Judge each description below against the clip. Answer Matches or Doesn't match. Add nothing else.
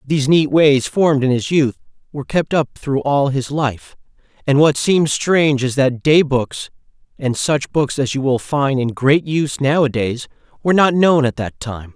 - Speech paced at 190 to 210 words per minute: Matches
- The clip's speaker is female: Doesn't match